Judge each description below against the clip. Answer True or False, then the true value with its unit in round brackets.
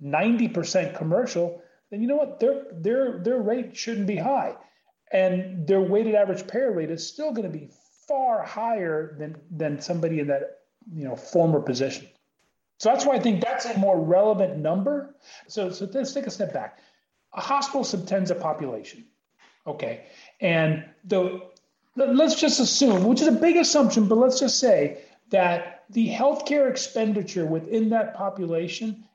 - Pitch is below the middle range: False (215 Hz)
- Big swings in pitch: True (6.8 semitones)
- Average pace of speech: True (160 wpm)